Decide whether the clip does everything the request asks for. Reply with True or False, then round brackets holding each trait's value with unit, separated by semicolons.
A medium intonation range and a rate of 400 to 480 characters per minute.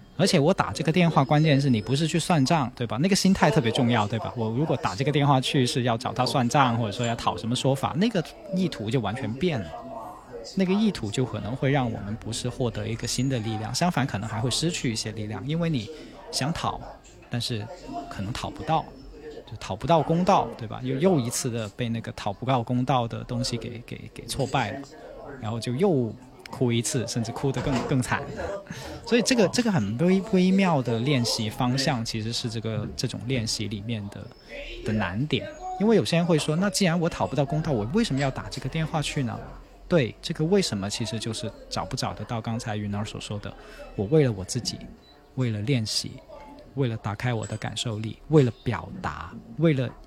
False (4.9 semitones; 305 characters per minute)